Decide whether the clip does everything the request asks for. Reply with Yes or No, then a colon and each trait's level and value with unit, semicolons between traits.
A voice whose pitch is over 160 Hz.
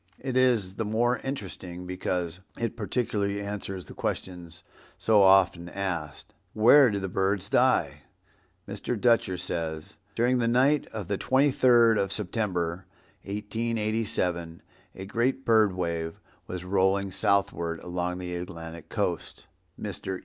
No: low, 100 Hz